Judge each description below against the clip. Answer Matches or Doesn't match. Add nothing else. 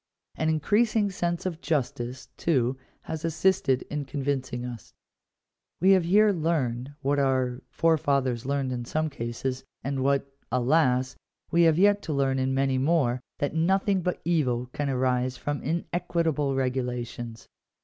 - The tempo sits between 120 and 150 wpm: Matches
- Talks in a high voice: Doesn't match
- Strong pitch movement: Doesn't match